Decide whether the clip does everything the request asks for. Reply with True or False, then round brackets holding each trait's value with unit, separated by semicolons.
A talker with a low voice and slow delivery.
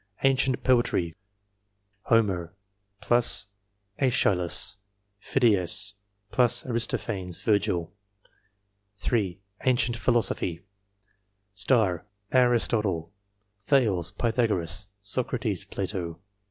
True (105 Hz; 55 wpm)